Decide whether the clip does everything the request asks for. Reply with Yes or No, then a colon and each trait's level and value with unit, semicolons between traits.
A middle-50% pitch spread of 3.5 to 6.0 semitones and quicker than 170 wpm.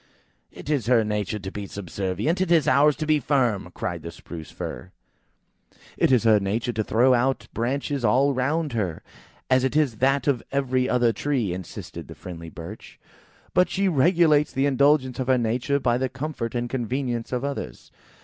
Yes: average, 4.5 semitones; average, 180 wpm